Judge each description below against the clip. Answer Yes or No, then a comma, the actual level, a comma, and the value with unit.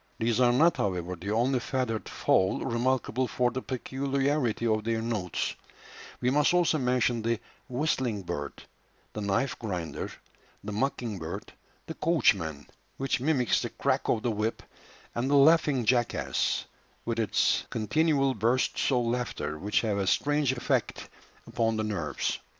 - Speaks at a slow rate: No, average, 145 wpm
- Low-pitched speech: Yes, low, 120 Hz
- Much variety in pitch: No, average, 3.7 semitones